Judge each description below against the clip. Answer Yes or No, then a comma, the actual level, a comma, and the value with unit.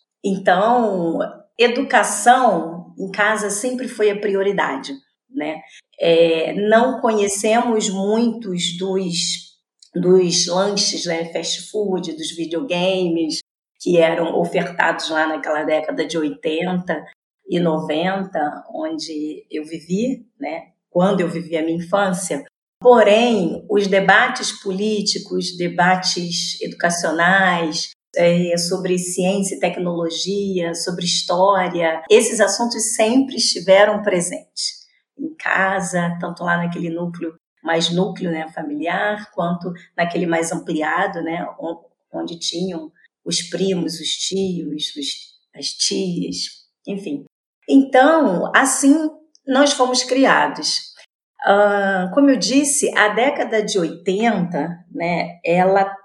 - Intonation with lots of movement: No, average, 4.1 semitones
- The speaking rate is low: Yes, slow, 105 wpm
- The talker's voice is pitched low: No, medium, 185 Hz